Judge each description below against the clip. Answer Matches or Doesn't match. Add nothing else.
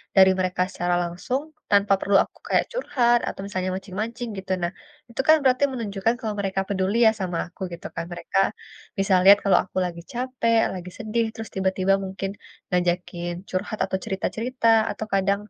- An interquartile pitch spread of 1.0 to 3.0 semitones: Doesn't match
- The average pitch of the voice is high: Matches